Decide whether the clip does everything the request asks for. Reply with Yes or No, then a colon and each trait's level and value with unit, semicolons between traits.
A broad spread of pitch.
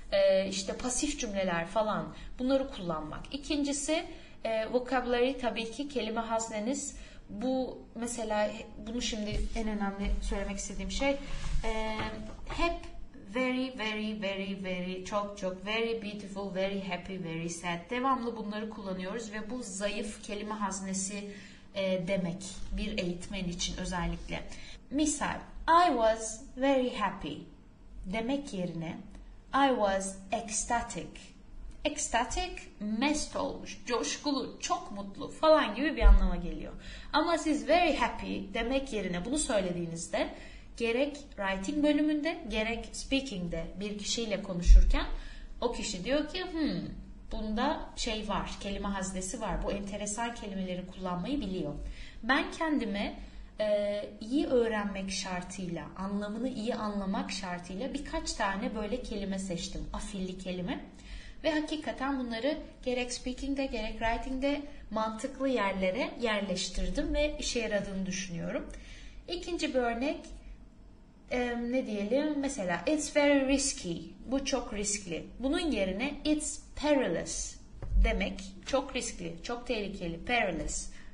Yes: wide, 5.7 semitones